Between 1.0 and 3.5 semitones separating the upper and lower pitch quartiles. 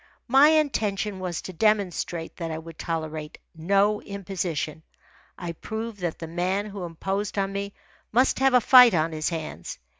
No: average, 4.2 semitones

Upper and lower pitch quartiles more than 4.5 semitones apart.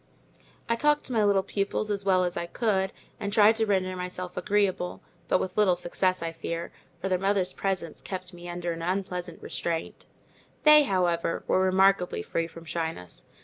No: narrow, 2.4 semitones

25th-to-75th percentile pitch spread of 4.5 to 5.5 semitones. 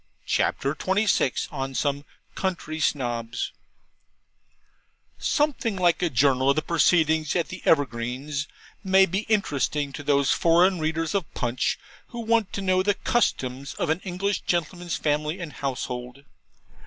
Yes: average, 5.2 semitones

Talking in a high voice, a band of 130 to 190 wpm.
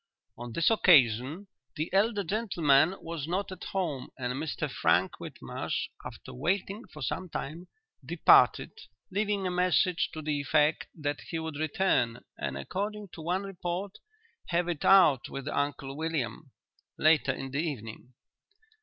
No: medium, 160 Hz; average, 145 wpm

